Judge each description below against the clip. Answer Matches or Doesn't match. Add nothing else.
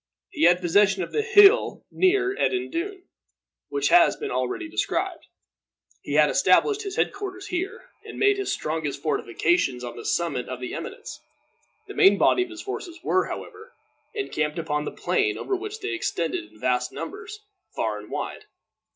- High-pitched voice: Matches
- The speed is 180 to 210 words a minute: Doesn't match